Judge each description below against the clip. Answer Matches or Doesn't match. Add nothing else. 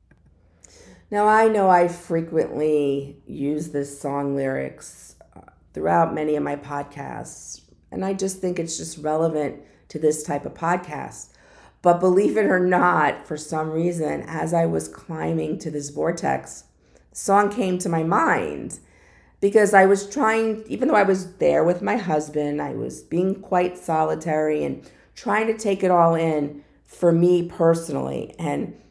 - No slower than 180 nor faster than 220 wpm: Doesn't match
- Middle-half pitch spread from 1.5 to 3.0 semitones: Doesn't match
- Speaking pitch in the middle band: Matches